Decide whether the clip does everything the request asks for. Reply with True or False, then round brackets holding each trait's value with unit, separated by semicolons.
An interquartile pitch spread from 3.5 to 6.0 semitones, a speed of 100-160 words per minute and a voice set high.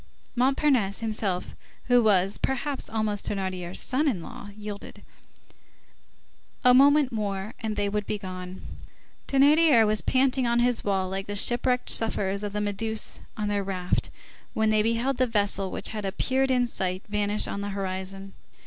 True (3.9 semitones; 155 wpm; 210 Hz)